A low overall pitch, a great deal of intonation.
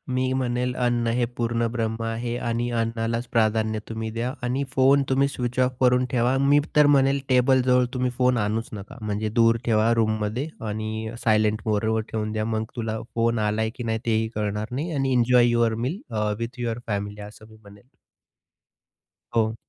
No: low, 115 Hz; narrow, 2.4 semitones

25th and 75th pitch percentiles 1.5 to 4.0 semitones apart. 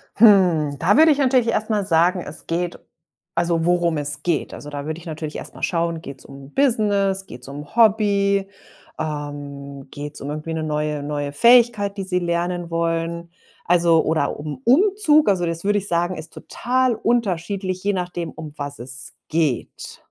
No: average, 4.9 semitones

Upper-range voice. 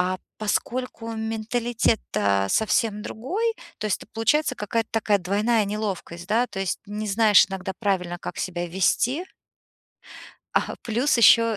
Yes: high, 215 Hz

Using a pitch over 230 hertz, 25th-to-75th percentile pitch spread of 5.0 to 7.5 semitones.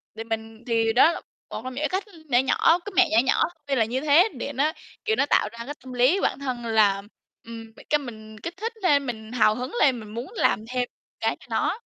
No: very high, 250 Hz; average, 4.5 semitones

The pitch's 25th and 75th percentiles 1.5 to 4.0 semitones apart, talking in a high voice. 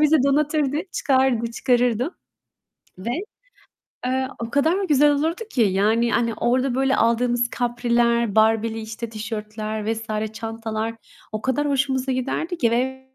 Yes: average, 3.0 semitones; high, 240 Hz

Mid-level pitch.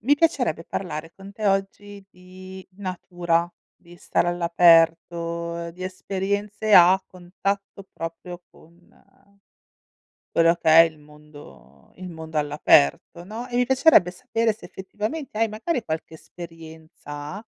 Yes: medium, 175 Hz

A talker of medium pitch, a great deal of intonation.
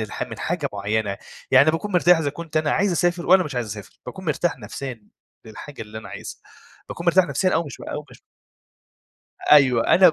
Yes: medium, 150 Hz; wide, 7.4 semitones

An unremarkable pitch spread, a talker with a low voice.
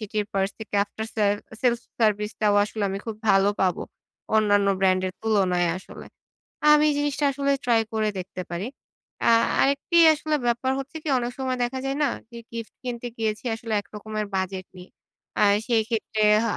No: average, 3.4 semitones; high, 220 Hz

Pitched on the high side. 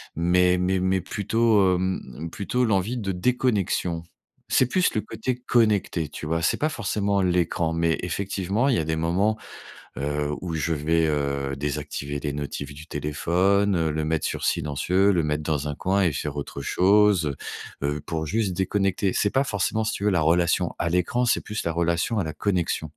No: very low, 90 Hz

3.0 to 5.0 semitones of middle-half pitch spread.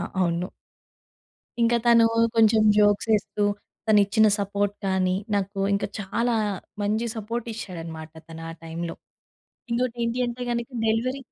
Yes: average, 3.7 semitones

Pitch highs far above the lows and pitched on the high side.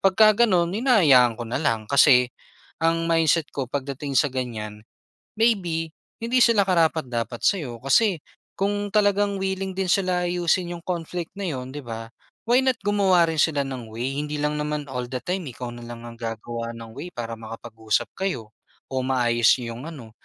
No: wide, 7.2 semitones; medium, 145 Hz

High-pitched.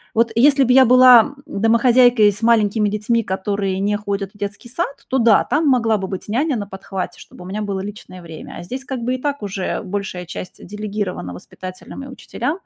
Yes: high, 210 Hz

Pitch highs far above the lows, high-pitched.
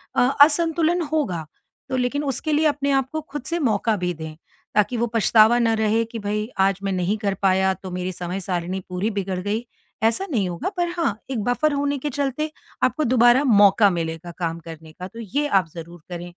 Yes: wide, 7.5 semitones; high, 215 Hz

